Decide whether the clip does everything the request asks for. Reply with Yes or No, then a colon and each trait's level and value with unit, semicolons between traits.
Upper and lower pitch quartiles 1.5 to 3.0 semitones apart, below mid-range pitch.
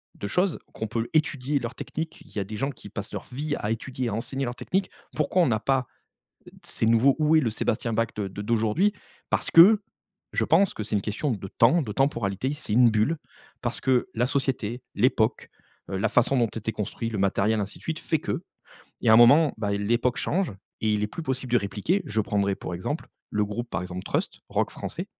No: average, 4.8 semitones; low, 115 Hz